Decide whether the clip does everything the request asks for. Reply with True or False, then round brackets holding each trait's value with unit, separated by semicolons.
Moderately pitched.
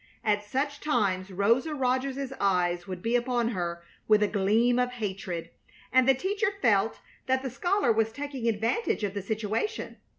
False (230 Hz)